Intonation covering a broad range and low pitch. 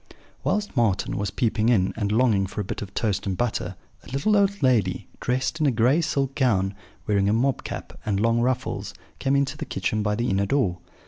No: average, 4.7 semitones; low, 115 Hz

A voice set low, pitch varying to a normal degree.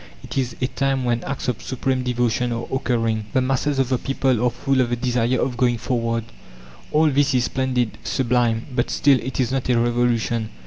No: low, 125 Hz; narrow, 1.8 semitones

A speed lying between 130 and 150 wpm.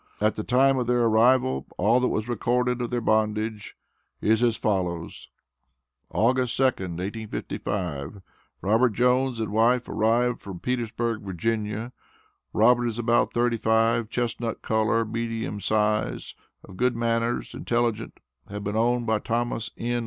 Yes: average, 140 wpm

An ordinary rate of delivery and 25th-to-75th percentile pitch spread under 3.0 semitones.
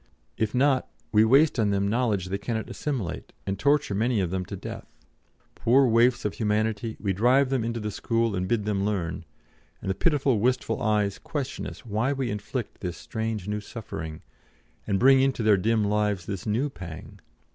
No: average, 185 wpm; average, 3.8 semitones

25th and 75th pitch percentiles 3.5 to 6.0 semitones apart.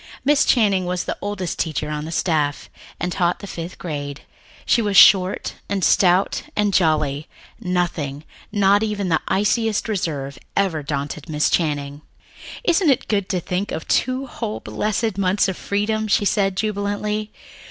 Yes: average, 4.7 semitones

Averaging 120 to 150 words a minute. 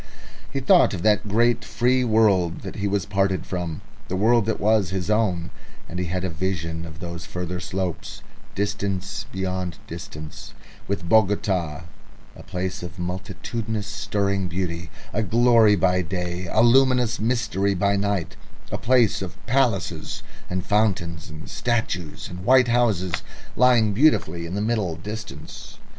Yes: average, 145 wpm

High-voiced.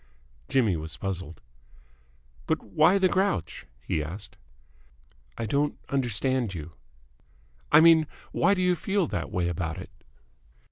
No: low, 115 Hz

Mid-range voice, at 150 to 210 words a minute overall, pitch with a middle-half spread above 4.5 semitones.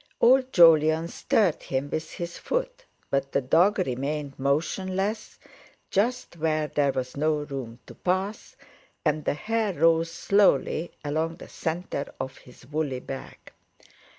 No: medium, 160 Hz; slow, 135 wpm; average, 5.2 semitones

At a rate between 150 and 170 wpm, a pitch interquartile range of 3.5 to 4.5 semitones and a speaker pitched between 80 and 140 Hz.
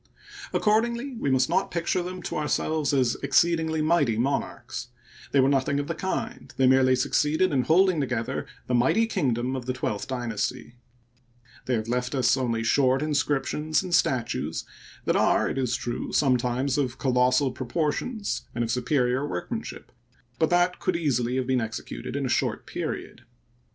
Yes: average, 160 wpm; average, 4.2 semitones; low, 135 Hz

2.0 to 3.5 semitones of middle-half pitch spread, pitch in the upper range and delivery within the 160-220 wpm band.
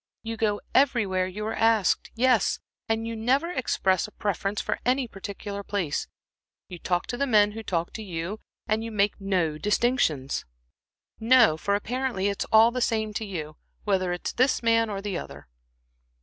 Yes: average, 3.2 semitones; high, 210 Hz; average, 175 wpm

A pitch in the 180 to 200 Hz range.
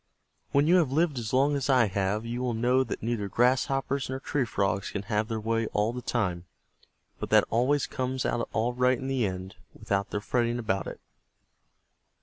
No: low, 120 Hz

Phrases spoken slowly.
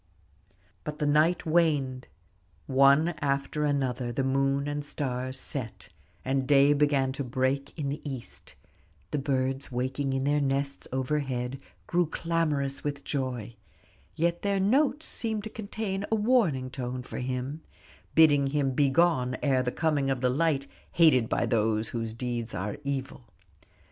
No: average, 145 wpm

